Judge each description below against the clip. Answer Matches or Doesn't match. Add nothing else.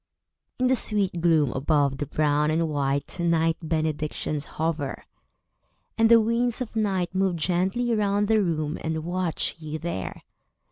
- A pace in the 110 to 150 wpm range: Matches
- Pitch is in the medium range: Matches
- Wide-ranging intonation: Doesn't match